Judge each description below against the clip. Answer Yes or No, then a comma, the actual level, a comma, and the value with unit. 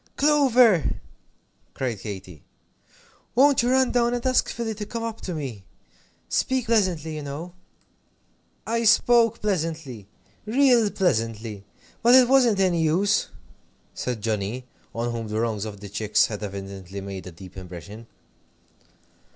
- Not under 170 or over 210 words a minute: No, slow, 135 wpm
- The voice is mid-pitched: Yes, medium, 155 Hz